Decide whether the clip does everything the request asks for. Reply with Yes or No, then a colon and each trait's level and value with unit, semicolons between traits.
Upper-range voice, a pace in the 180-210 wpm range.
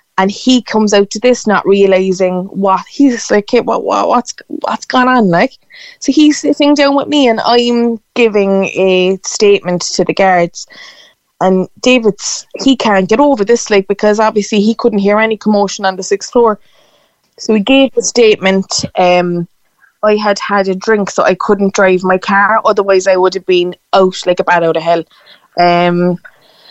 Yes: high, 205 Hz; average, 185 wpm